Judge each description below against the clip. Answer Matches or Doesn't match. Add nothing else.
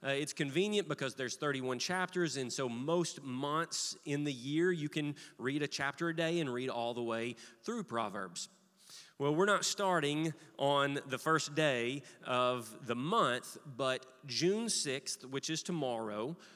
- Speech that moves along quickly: Doesn't match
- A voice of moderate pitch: Matches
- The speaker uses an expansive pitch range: Doesn't match